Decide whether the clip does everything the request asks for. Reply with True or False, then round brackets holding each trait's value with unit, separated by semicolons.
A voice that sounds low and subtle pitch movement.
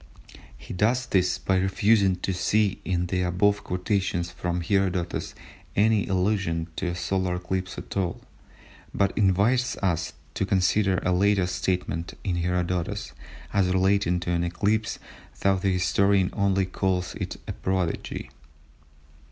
True (95 Hz; 1.9 semitones)